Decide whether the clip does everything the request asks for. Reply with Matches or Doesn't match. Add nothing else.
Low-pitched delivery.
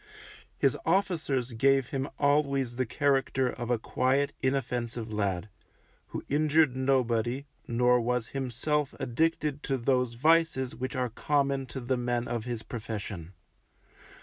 Matches